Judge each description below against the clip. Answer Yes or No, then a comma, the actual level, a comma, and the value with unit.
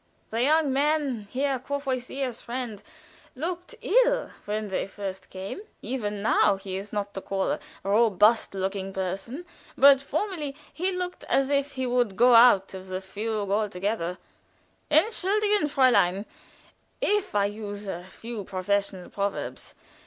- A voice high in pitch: Yes, high, 225 Hz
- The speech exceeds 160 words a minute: No, average, 140 wpm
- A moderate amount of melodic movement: No, wide, 6.1 semitones